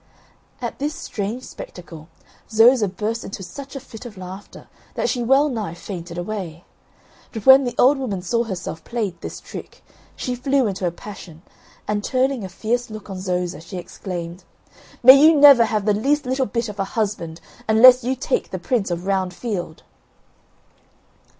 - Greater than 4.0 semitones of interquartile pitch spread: Yes, wide, 5.4 semitones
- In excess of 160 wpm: Yes, average, 170 wpm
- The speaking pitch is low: No, high, 215 Hz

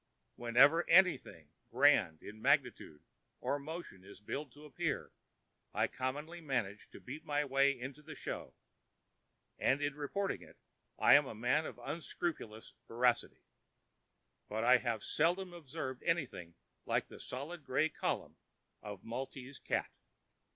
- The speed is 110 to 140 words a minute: Yes, slow, 135 wpm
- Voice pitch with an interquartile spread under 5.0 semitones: Yes, average, 4.3 semitones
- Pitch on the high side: No, low, 135 Hz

